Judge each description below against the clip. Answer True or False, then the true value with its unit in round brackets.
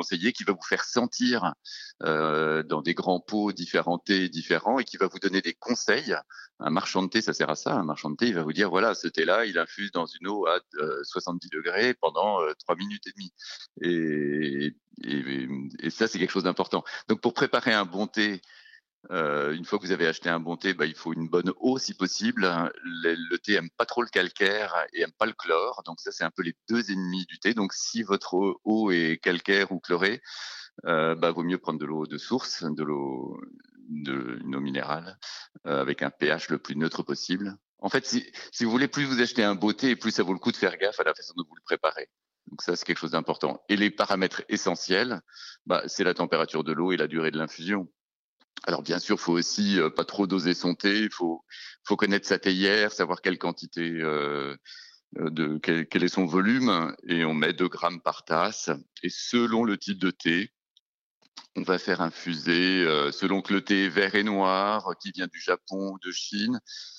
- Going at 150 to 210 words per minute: False (220 wpm)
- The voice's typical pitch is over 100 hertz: False (95 Hz)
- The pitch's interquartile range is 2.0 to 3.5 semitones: False (4.6 semitones)